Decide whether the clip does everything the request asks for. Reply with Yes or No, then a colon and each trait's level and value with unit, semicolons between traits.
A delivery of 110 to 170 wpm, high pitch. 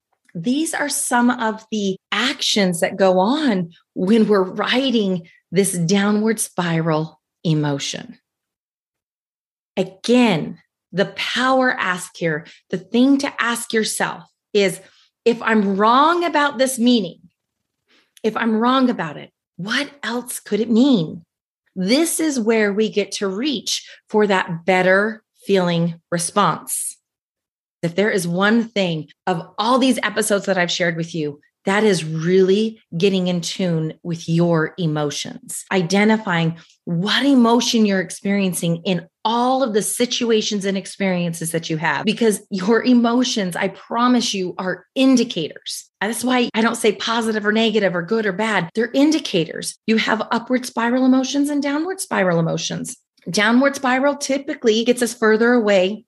Yes: average, 140 wpm; high, 210 Hz